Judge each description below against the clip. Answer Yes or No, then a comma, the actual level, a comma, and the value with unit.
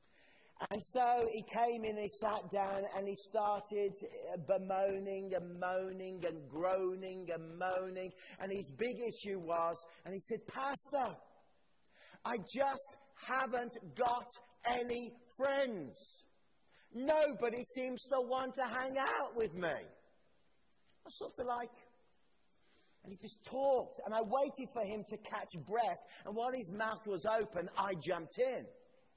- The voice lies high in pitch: Yes, high, 220 Hz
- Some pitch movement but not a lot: Yes, average, 4.6 semitones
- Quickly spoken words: No, average, 140 wpm